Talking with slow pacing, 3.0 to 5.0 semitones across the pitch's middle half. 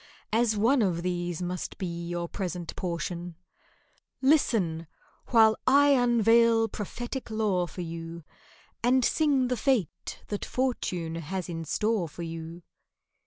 No: slow, 125 wpm; wide, 5.6 semitones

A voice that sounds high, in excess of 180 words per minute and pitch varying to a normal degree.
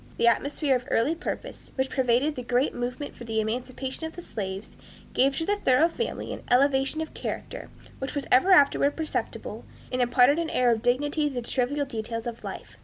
Yes: very high, 265 Hz; average, 195 wpm; average, 3.2 semitones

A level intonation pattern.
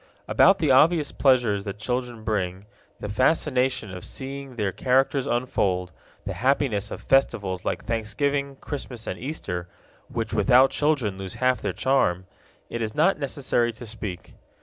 No: average, 4.9 semitones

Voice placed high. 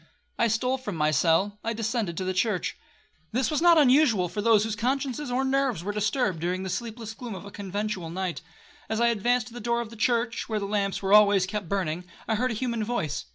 Yes: high, 215 Hz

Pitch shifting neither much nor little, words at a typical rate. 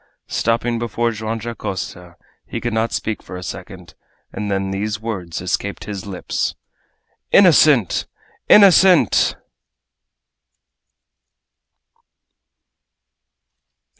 No: average, 3.4 semitones; slow, 85 wpm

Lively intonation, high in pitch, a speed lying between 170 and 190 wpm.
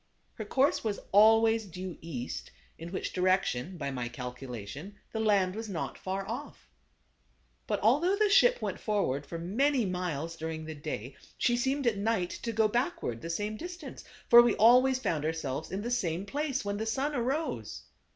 Yes: wide, 6.7 semitones; high, 205 Hz; average, 180 wpm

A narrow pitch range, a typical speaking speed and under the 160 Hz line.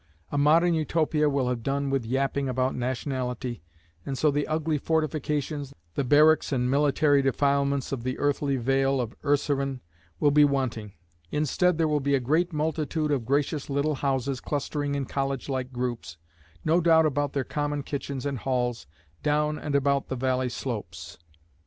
Yes: narrow, 2.3 semitones; average, 165 wpm; medium, 140 Hz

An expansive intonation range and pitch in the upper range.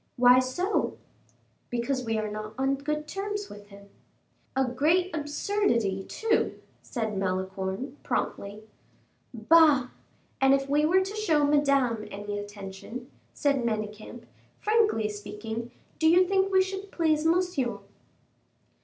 Yes: wide, 7.5 semitones; very high, 265 Hz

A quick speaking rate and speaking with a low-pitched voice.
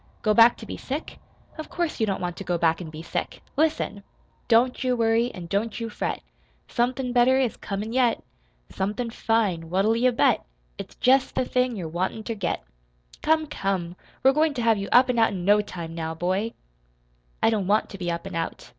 No: fast, 210 wpm; high, 220 Hz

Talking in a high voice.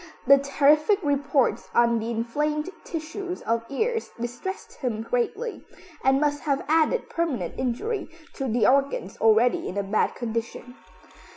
Yes: very high, 275 Hz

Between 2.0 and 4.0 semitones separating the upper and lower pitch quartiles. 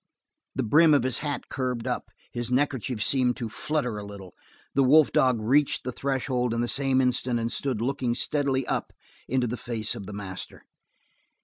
Yes: narrow, 2.6 semitones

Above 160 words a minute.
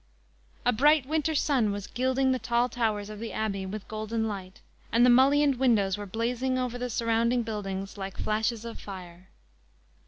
Yes: average, 175 wpm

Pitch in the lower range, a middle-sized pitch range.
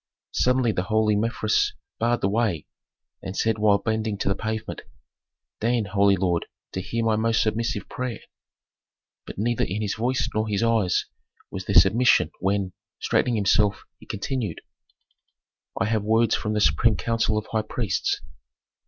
No: low, 110 Hz; narrow, 2.3 semitones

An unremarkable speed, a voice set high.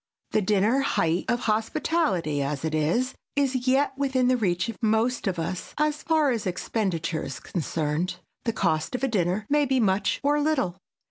Yes: average, 180 wpm; high, 220 Hz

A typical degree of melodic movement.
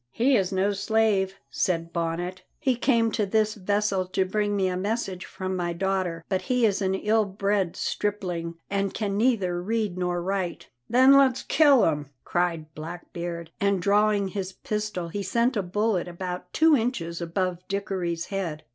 Yes: average, 3.1 semitones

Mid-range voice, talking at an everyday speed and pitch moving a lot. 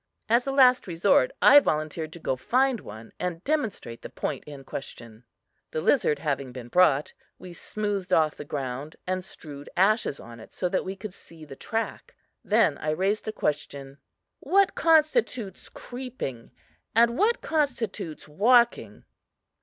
Yes: medium, 180 Hz; average, 155 wpm; wide, 8.6 semitones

